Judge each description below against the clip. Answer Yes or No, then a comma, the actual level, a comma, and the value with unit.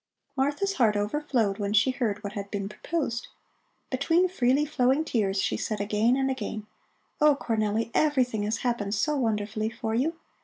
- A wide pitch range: No, average, 4.8 semitones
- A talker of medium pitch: No, high, 230 Hz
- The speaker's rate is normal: Yes, average, 160 wpm